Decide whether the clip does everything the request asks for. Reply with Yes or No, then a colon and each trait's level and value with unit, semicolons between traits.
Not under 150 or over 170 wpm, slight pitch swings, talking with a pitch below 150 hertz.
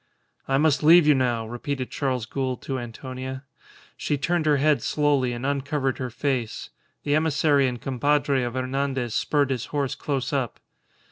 Yes: average, 160 wpm; narrow, 2.2 semitones; low, 135 Hz